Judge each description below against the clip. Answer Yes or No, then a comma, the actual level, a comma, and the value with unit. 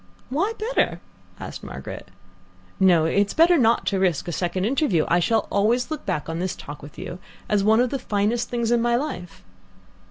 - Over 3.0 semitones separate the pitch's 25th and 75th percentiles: Yes, wide, 5.6 semitones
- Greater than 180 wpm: Yes, average, 195 wpm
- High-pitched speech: Yes, high, 210 Hz